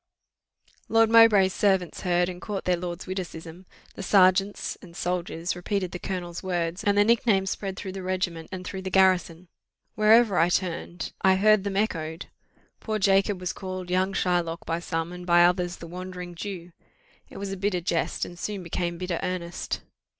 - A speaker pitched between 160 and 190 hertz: Yes, medium, 185 Hz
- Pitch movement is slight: Yes, narrow, 1.9 semitones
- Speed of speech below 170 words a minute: No, average, 180 wpm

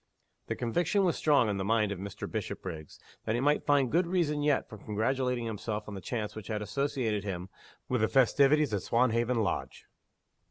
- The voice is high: No, low, 115 Hz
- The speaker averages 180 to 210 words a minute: Yes, average, 190 wpm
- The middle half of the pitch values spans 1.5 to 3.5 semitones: No, average, 5.0 semitones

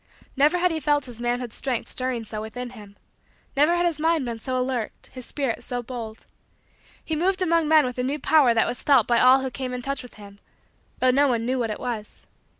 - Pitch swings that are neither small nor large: Yes, average, 3.6 semitones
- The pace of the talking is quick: Yes, fast, 230 wpm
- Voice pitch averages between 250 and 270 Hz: Yes, very high, 255 Hz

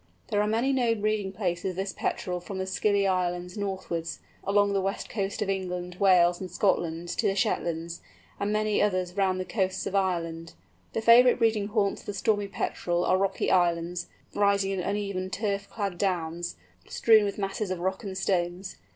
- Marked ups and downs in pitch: No, narrow, 2.4 semitones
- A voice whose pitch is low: No, high, 190 Hz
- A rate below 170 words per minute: No, average, 185 wpm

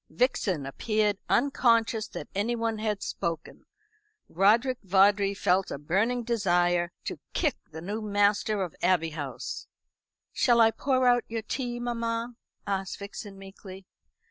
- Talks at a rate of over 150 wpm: No, slow, 135 wpm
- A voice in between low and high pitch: No, high, 205 Hz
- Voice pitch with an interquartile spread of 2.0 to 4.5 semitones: Yes, average, 3.4 semitones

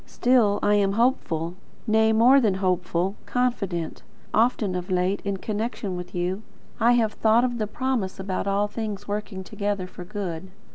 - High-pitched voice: Yes, high, 205 Hz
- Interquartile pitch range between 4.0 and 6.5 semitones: No, average, 3.1 semitones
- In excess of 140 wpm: Yes, average, 160 wpm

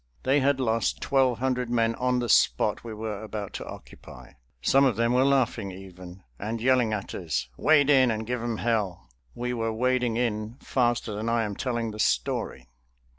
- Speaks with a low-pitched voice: Yes, low, 115 Hz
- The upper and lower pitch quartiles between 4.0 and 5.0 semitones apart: No, average, 2.8 semitones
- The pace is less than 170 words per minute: No, average, 185 wpm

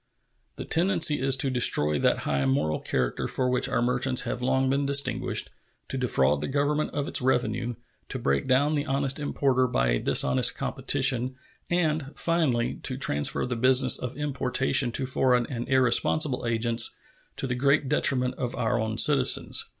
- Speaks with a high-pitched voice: No, low, 130 Hz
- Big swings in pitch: No, average, 2.7 semitones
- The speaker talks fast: No, average, 165 wpm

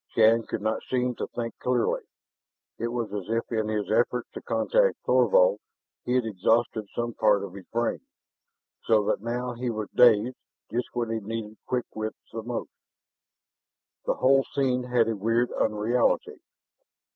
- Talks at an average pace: Yes, average, 160 wpm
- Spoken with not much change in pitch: Yes, narrow, 2.2 semitones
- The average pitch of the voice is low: Yes, low, 115 Hz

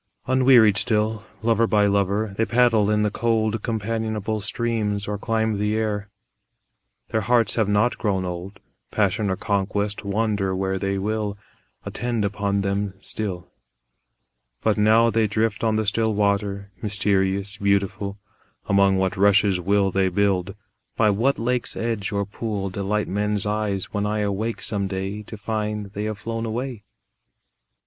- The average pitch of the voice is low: Yes, low, 105 Hz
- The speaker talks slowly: No, average, 150 wpm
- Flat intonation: Yes, narrow, 1.8 semitones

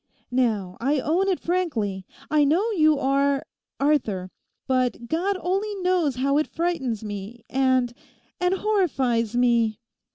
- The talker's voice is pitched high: Yes, very high, 275 Hz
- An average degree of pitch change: No, wide, 6.7 semitones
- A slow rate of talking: Yes, slow, 110 wpm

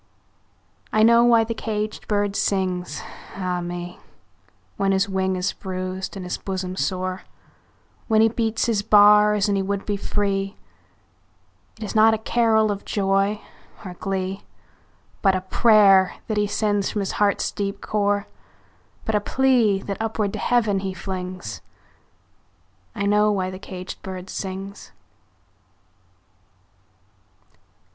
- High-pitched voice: Yes, high, 200 Hz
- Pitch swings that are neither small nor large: No, narrow, 2.1 semitones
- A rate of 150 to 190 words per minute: No, slow, 135 wpm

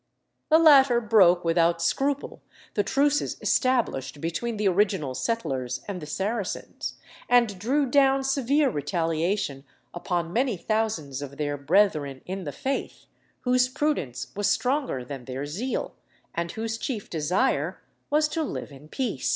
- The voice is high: Yes, high, 200 Hz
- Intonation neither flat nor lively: No, wide, 8.9 semitones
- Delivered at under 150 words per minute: Yes, average, 140 wpm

